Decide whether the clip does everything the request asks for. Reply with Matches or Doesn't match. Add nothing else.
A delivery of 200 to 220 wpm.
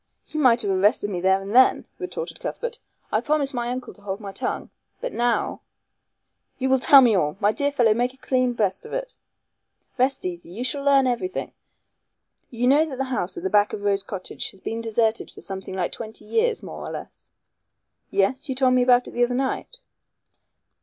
Matches